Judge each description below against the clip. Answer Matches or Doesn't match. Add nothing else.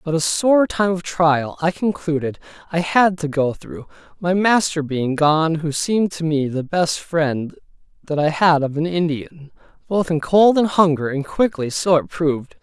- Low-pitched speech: Doesn't match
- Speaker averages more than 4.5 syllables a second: Doesn't match